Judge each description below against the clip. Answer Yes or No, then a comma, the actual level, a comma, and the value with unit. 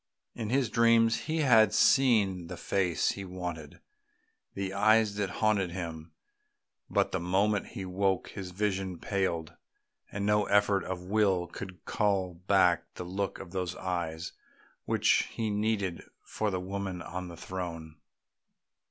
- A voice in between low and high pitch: No, very low, 95 Hz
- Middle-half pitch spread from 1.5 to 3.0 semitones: Yes, average, 2.7 semitones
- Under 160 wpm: Yes, average, 145 wpm